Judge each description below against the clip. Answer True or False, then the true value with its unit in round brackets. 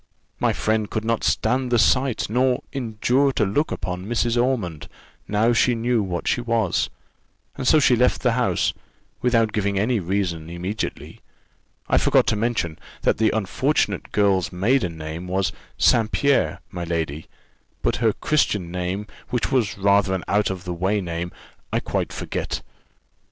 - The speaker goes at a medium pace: True (160 wpm)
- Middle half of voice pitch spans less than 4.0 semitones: False (4.9 semitones)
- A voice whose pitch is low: True (105 Hz)